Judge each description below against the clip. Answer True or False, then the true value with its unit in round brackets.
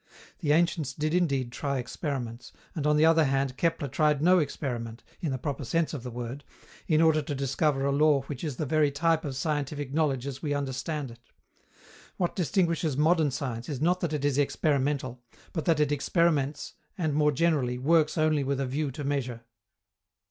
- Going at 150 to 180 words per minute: False (190 wpm)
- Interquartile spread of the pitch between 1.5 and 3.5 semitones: True (2.6 semitones)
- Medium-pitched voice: True (145 Hz)